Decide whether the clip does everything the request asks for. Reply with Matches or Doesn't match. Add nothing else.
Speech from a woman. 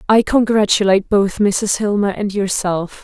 Matches